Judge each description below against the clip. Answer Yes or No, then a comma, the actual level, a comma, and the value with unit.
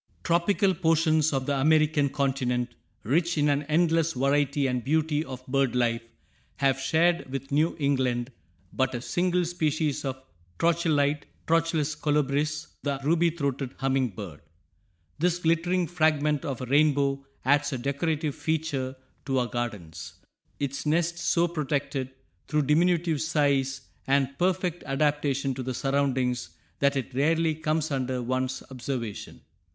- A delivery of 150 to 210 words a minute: No, slow, 135 wpm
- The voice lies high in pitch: No, medium, 145 Hz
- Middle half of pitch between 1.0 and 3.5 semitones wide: Yes, average, 3.2 semitones